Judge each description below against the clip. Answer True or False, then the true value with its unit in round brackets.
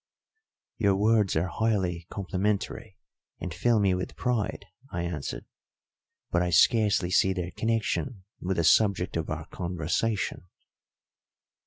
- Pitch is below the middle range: True (95 Hz)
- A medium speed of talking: False (125 wpm)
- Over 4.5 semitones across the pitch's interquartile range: False (3.4 semitones)